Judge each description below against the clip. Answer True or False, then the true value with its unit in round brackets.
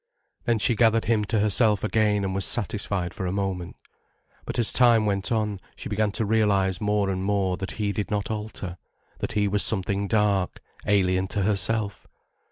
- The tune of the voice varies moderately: False (1.9 semitones)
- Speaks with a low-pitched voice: True (105 Hz)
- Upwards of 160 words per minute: True (180 wpm)